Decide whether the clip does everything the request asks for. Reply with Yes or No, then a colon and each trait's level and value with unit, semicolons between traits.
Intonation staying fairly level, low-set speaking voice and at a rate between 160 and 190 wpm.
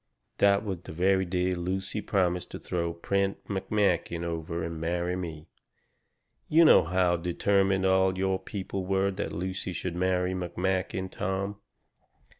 No: narrow, 1.7 semitones; very low, 95 Hz; average, 140 wpm